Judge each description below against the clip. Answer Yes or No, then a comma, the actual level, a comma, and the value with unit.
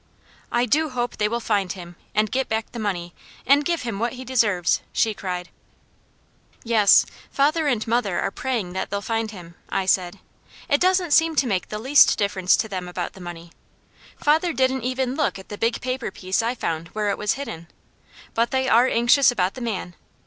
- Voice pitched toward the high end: Yes, high, 225 Hz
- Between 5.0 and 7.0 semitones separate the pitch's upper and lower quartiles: Yes, wide, 5.4 semitones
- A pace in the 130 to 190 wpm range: No, average, 200 wpm